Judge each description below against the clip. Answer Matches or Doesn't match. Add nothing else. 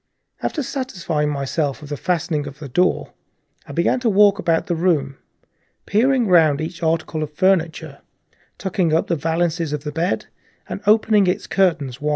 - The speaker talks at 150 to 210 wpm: Matches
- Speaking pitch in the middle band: Matches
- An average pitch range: Matches